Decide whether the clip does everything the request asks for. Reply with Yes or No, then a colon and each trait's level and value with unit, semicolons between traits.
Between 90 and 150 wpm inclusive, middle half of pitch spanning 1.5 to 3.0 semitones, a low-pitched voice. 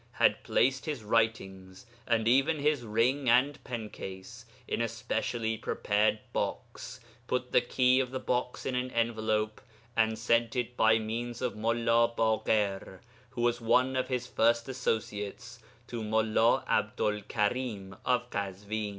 Yes: average, 145 wpm; narrow, 2.4 semitones; low, 115 Hz